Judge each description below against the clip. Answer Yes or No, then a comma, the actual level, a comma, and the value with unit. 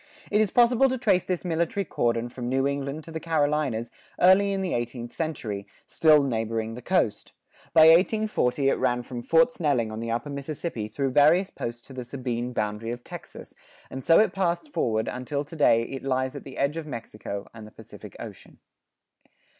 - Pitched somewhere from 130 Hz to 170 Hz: Yes, medium, 140 Hz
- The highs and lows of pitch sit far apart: Yes, wide, 5.8 semitones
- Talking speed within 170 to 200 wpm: Yes, average, 190 wpm